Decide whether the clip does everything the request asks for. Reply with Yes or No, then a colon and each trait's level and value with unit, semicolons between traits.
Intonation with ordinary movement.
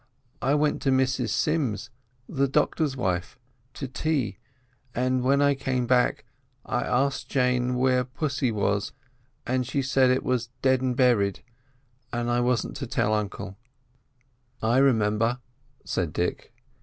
No: narrow, 2.3 semitones